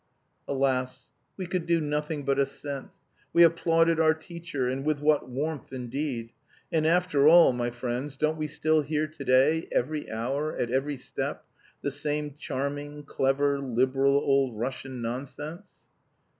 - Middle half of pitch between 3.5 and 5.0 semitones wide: No, average, 2.9 semitones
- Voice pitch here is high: No, medium, 145 Hz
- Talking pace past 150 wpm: No, average, 145 wpm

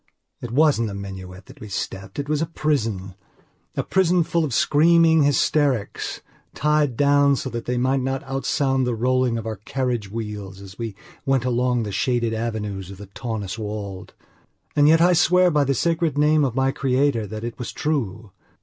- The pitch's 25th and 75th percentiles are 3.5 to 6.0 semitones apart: Yes, average, 5.1 semitones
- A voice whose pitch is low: Yes, low, 125 Hz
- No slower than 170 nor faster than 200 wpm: Yes, average, 180 wpm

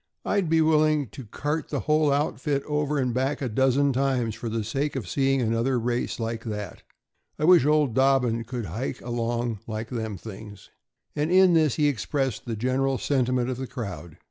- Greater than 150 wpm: Yes, average, 185 wpm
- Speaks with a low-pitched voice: Yes, low, 130 Hz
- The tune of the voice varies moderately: Yes, average, 4.1 semitones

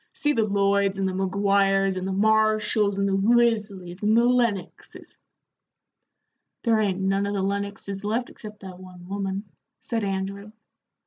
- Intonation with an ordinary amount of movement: No, narrow, 1.9 semitones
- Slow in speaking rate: No, average, 155 wpm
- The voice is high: Yes, high, 200 Hz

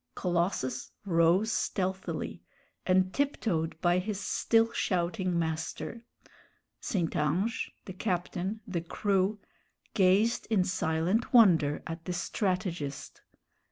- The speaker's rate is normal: No, slow, 100 wpm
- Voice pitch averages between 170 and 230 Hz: Yes, medium, 185 Hz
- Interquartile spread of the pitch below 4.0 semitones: Yes, average, 3.5 semitones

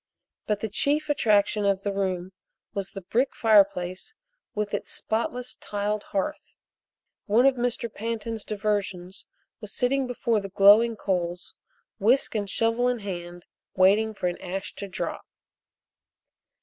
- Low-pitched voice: No, high, 210 Hz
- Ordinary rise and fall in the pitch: Yes, average, 3.0 semitones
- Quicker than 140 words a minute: No, slow, 135 wpm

